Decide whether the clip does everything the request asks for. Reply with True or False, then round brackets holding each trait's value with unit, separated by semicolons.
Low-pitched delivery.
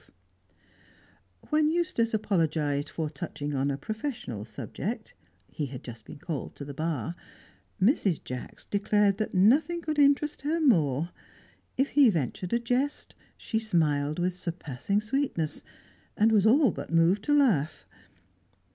False (190 Hz)